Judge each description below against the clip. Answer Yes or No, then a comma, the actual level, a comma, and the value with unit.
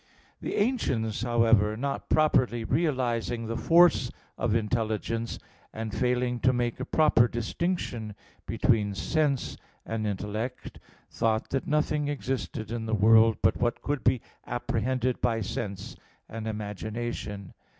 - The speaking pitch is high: No, low, 115 Hz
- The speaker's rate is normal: No, slow, 125 wpm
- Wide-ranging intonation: No, average, 2.7 semitones